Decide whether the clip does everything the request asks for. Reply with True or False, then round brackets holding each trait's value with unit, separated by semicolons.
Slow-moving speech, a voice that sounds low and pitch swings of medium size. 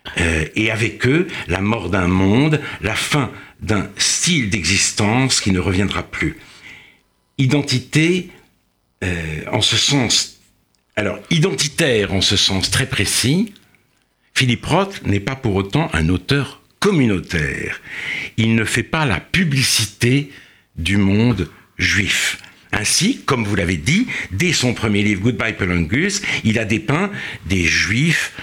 False (130 wpm; 115 Hz; 6.3 semitones)